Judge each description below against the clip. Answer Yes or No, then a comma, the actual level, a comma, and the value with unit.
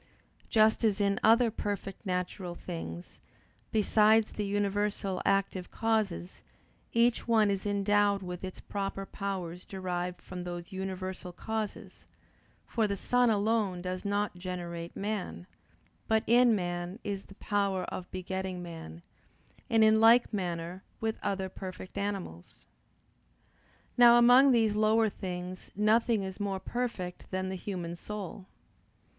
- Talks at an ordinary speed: No, slow, 130 wpm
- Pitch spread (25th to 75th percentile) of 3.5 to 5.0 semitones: No, average, 2.9 semitones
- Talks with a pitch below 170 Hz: No, high, 195 Hz